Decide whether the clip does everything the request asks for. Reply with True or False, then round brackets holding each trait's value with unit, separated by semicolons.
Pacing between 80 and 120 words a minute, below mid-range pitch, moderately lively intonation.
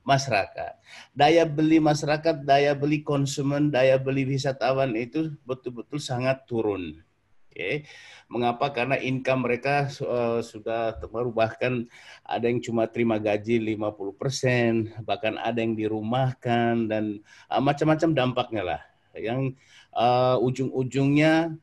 True (110 wpm; 125 Hz; 3.5 semitones)